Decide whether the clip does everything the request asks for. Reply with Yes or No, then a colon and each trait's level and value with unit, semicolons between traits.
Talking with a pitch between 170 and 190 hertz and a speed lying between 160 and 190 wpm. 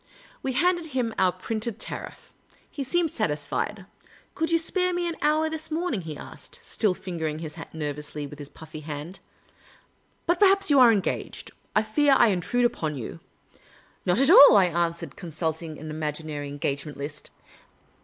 Yes: medium, 185 Hz; average, 180 wpm